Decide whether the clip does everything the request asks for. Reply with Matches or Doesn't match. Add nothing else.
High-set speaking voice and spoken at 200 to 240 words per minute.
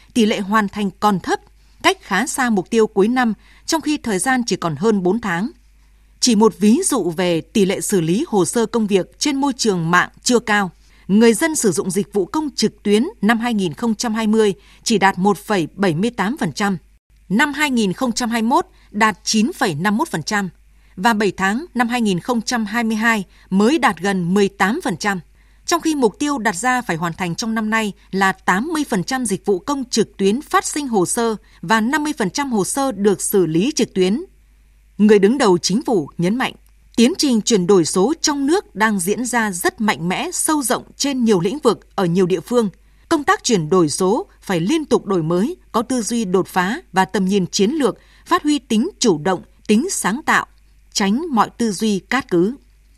Doesn't match